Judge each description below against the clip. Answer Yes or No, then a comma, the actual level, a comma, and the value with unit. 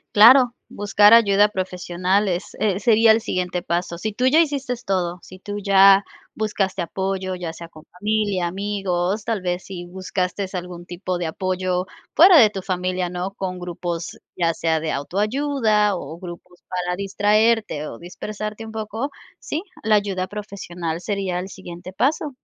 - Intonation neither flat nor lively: Yes, average, 3.0 semitones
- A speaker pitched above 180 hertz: Yes, high, 190 Hz